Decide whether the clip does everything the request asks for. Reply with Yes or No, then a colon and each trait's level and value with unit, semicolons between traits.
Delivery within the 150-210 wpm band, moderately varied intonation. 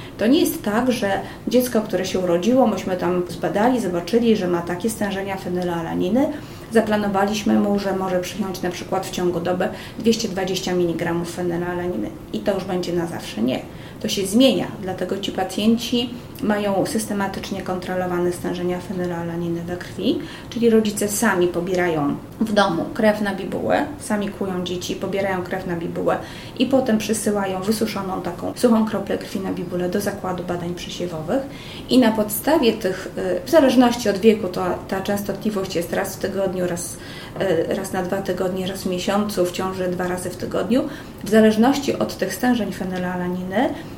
Yes: average, 155 wpm; average, 3.5 semitones